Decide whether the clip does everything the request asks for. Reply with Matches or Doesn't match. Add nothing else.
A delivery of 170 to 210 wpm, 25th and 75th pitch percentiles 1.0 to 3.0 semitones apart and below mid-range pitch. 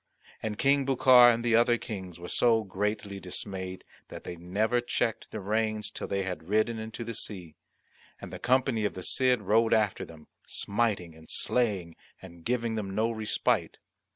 Doesn't match